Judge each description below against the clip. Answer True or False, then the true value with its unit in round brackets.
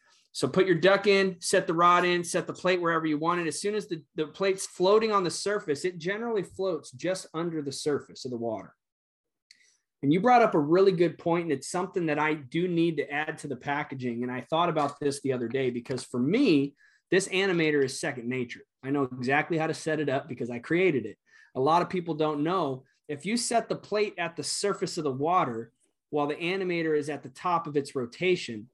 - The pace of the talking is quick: True (230 wpm)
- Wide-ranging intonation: False (4.6 semitones)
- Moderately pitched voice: True (160 Hz)